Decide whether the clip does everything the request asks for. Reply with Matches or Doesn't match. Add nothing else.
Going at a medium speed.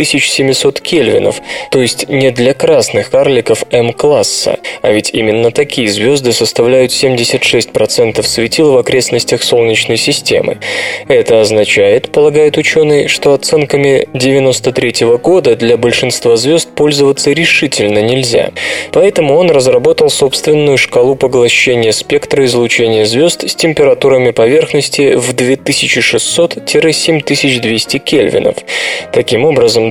Doesn't match